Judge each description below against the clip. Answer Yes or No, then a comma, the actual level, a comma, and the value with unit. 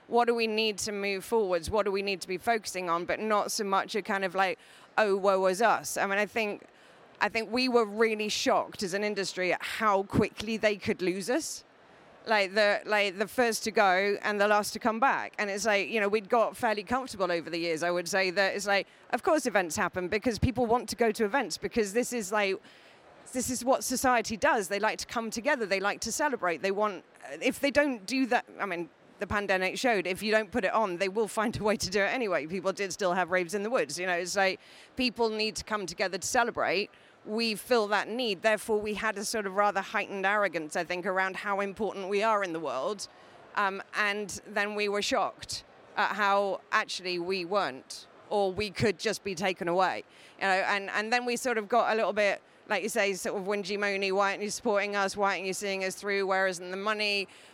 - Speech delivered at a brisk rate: Yes, fast, 240 wpm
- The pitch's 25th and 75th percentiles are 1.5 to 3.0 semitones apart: Yes, narrow, 2.4 semitones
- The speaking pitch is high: Yes, high, 205 Hz